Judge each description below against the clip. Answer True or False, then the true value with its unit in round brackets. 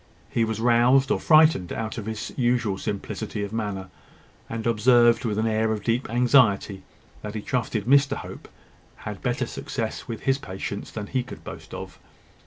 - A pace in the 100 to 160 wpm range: False (175 wpm)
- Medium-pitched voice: False (115 Hz)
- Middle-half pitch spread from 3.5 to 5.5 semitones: False (2.8 semitones)